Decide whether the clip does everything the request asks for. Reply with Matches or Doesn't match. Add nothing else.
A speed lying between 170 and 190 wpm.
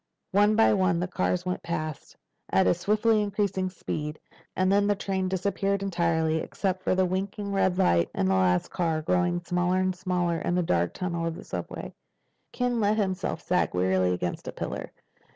Matches